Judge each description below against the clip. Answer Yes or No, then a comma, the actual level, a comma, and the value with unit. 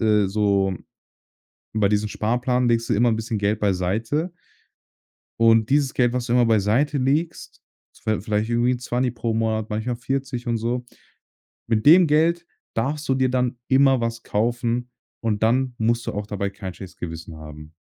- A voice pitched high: No, low, 115 Hz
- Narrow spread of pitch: No, average, 3.1 semitones